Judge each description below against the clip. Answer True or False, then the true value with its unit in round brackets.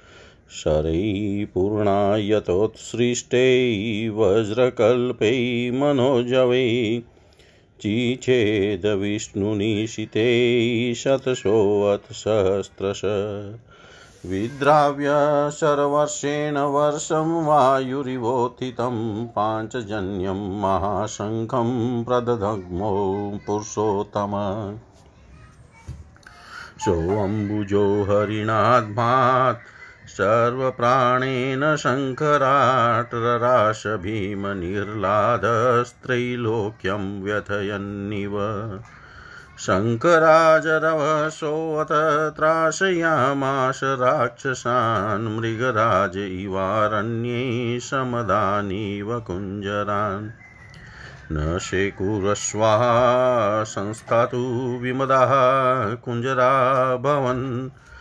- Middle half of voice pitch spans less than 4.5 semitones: True (3.9 semitones)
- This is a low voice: True (115 Hz)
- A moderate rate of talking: False (35 wpm)